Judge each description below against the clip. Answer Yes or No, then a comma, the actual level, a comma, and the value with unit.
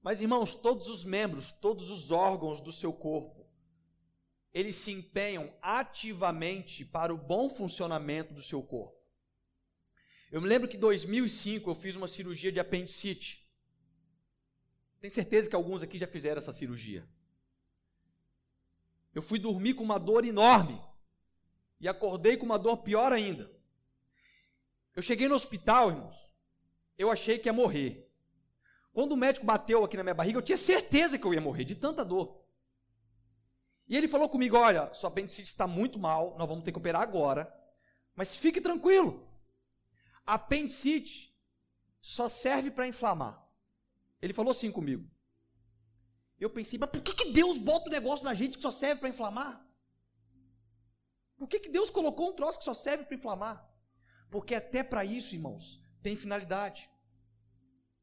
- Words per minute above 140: Yes, average, 155 wpm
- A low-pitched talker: No, high, 190 Hz